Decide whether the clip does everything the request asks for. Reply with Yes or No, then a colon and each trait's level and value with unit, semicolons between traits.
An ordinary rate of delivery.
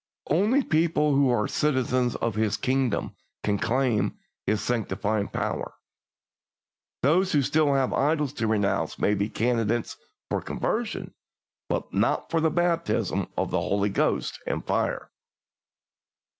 No: slow, 130 wpm